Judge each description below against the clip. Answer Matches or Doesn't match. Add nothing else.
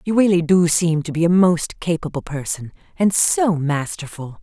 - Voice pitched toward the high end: Doesn't match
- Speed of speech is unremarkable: Matches